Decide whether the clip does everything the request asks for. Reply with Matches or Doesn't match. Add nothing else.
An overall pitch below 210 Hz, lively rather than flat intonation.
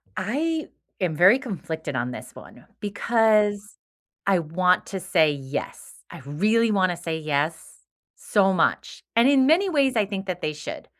Matches